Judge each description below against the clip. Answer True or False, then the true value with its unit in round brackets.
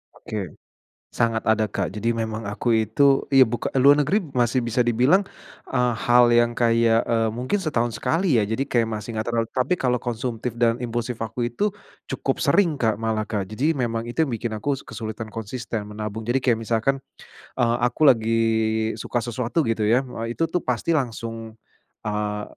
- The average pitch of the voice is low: True (115 Hz)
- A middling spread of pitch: False (2.1 semitones)